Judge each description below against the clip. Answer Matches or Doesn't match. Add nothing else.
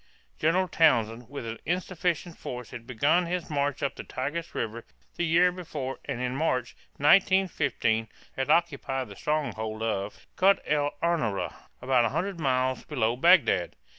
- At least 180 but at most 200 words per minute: Doesn't match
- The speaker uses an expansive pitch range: Matches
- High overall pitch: Doesn't match